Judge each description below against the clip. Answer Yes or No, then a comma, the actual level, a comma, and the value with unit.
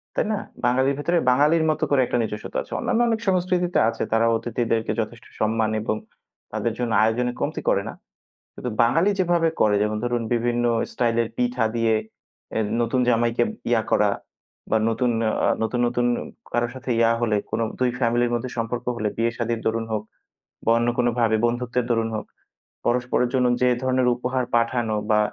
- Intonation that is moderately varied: No, narrow, 1.9 semitones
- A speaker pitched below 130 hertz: Yes, low, 120 Hz